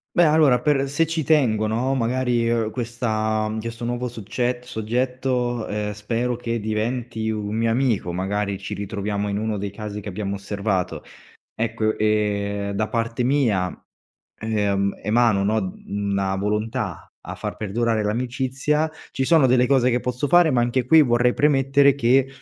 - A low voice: Yes, low, 115 Hz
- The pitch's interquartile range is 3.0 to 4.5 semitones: Yes, average, 3.3 semitones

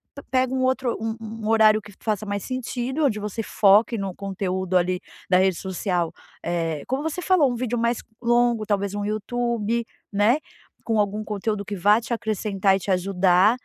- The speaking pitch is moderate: No, high, 215 Hz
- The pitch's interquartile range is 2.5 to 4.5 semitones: Yes, average, 3.4 semitones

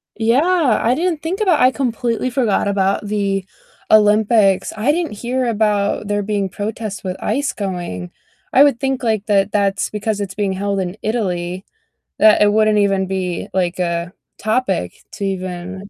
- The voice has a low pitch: No, high, 205 Hz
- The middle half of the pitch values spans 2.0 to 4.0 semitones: Yes, average, 3.4 semitones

